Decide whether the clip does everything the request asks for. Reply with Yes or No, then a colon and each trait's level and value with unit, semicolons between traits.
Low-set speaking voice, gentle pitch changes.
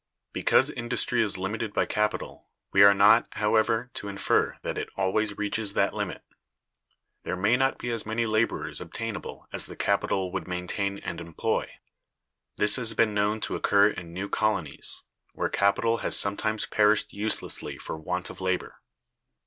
Yes: low, 105 Hz; narrow, 2.2 semitones